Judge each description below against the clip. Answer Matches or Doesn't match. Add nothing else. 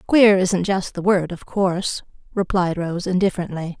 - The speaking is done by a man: Doesn't match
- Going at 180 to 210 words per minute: Doesn't match